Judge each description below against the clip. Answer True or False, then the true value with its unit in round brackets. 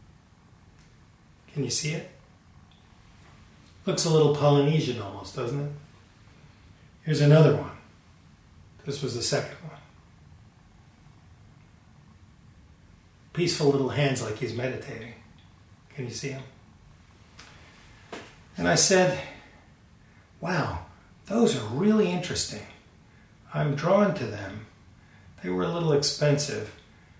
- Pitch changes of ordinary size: False (6.7 semitones)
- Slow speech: True (100 wpm)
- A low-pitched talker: True (120 Hz)